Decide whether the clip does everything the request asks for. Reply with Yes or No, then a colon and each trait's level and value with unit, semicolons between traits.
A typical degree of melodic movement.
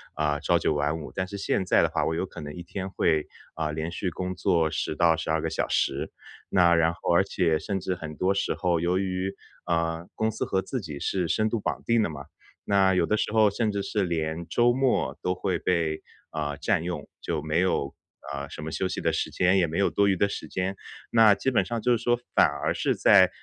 Yes: average, 3.4 semitones